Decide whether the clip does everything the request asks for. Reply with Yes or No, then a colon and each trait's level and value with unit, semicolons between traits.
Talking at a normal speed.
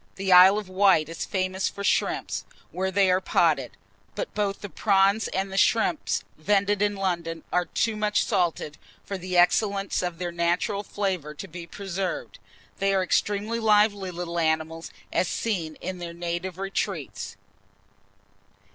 Yes: average, 155 wpm